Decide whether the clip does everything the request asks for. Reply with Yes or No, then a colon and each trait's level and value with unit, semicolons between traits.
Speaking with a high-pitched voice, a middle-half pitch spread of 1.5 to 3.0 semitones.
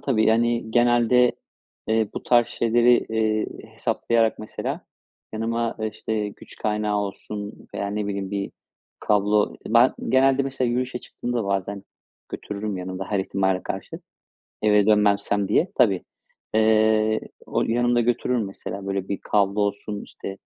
No: low, 110 Hz; narrow, 2.6 semitones